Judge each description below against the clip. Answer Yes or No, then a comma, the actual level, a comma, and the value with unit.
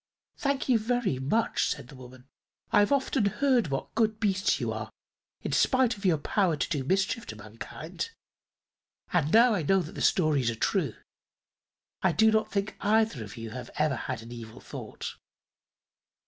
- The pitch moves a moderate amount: No, wide, 8.9 semitones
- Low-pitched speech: No, high, 190 Hz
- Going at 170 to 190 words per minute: Yes, average, 175 wpm